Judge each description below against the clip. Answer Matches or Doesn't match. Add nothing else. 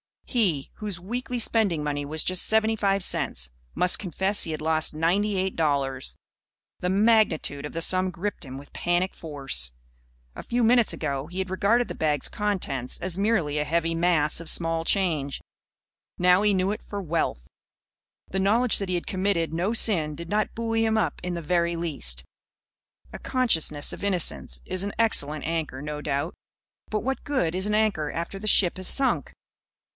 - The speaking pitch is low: Doesn't match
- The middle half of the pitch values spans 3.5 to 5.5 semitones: Matches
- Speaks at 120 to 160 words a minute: Doesn't match